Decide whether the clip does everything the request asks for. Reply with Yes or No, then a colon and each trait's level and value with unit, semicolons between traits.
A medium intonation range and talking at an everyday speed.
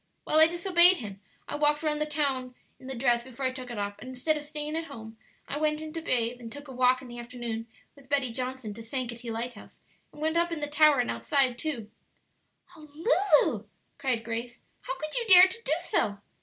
No: average, 4.3 semitones; fast, 225 wpm